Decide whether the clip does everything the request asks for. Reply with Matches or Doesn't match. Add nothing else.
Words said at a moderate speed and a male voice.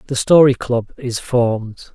Matches